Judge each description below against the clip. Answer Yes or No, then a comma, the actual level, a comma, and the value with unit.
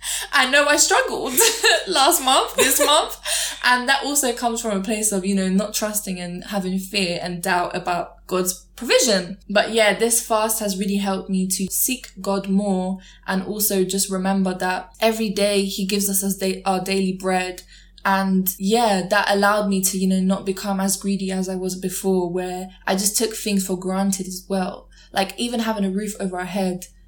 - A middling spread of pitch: No, narrow, 2.0 semitones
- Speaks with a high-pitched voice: Yes, high, 195 Hz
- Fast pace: No, average, 195 wpm